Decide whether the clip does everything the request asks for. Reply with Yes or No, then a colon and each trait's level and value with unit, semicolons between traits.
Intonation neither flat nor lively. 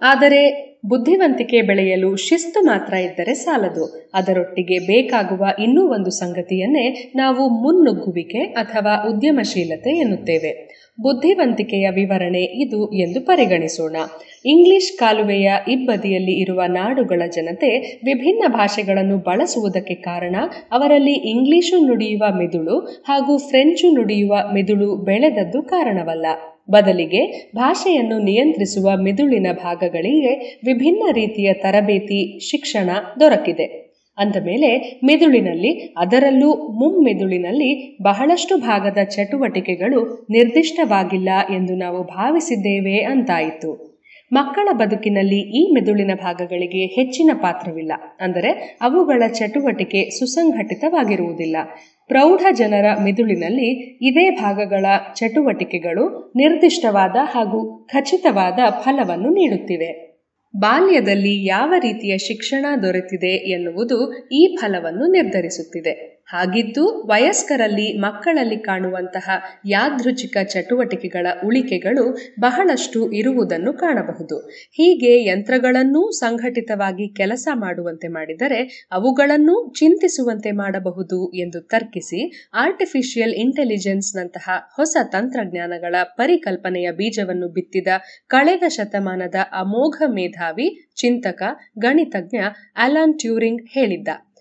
No: wide, 6.7 semitones